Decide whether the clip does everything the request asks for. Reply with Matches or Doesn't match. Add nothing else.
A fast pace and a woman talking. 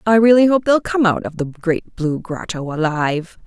Matches